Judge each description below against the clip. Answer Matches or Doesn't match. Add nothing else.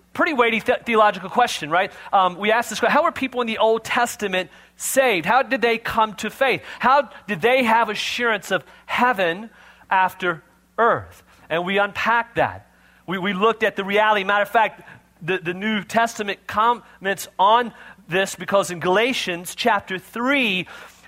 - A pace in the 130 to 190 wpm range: Matches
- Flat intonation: Doesn't match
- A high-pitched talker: Matches